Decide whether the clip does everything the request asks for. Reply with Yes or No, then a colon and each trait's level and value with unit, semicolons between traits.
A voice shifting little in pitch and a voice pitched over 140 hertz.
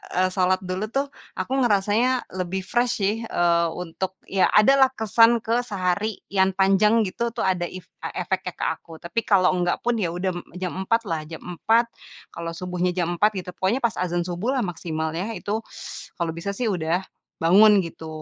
No: average, 3.6 semitones; high, 190 Hz